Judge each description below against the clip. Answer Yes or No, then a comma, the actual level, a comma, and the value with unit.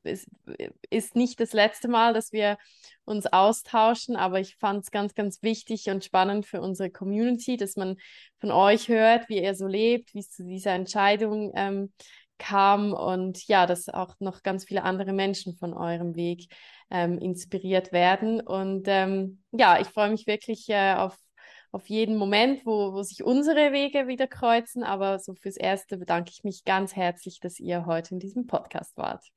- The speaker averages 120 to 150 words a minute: No, average, 180 wpm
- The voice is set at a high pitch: Yes, high, 195 Hz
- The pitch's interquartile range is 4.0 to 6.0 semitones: No, average, 2.7 semitones